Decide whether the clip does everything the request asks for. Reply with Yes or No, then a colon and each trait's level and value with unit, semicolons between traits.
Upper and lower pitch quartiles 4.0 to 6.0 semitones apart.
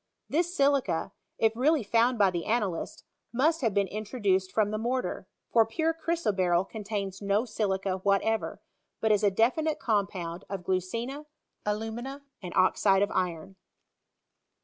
Yes: average, 4.3 semitones